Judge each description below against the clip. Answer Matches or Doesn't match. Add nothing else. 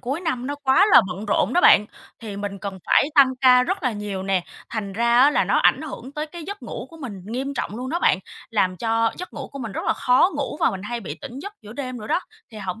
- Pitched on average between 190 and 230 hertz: Doesn't match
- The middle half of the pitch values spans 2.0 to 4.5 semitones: Doesn't match